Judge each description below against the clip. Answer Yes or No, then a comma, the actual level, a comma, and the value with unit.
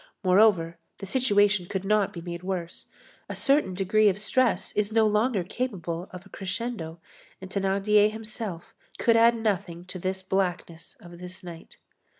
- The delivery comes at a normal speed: Yes, average, 160 wpm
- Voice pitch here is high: Yes, high, 195 Hz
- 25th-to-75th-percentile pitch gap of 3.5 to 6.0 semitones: No, average, 3.1 semitones